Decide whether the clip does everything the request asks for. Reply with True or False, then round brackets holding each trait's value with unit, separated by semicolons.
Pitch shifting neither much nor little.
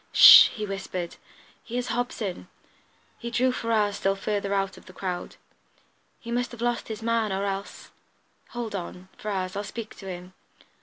True (3.3 semitones)